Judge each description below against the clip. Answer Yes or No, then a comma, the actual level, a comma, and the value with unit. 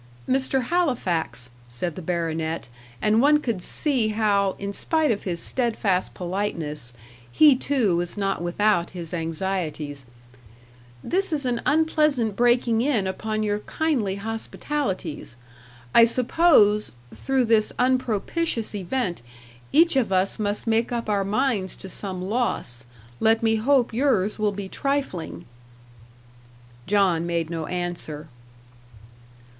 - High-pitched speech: Yes, high, 210 Hz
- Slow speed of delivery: Yes, slow, 125 wpm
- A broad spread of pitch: Yes, wide, 6.0 semitones